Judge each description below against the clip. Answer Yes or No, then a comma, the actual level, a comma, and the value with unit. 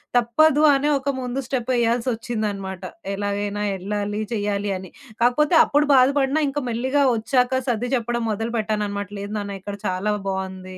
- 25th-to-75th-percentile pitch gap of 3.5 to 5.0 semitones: Yes, average, 4.0 semitones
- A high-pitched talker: Yes, high, 225 Hz